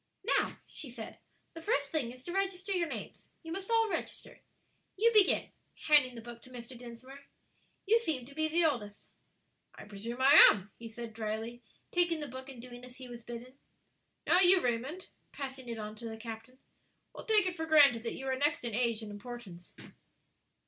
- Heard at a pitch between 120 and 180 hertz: No, very high, 255 Hz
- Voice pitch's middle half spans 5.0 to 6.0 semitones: Yes, wide, 5.6 semitones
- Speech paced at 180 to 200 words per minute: Yes, average, 195 wpm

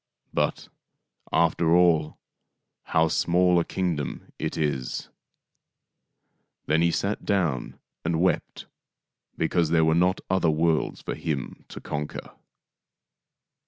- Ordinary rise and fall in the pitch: No, narrow, 2.2 semitones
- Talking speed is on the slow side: Yes, slow, 115 wpm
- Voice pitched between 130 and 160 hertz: No, very low, 80 Hz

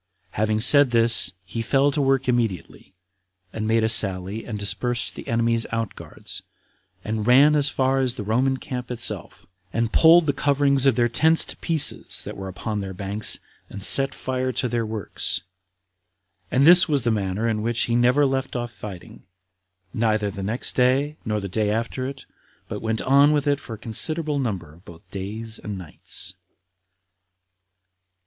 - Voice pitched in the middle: No, low, 115 Hz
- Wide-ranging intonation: No, average, 4.0 semitones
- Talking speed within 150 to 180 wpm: Yes, average, 175 wpm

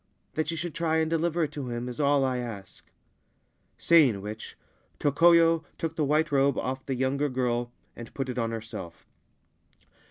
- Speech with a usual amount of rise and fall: Yes, average, 4.6 semitones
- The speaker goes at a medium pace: Yes, average, 170 wpm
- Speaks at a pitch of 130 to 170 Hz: Yes, medium, 140 Hz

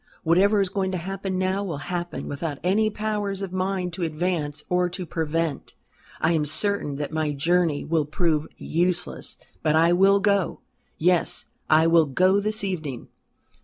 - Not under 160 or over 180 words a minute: Yes, average, 165 wpm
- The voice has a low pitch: No, medium, 175 Hz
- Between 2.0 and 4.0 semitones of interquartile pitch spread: Yes, average, 3.4 semitones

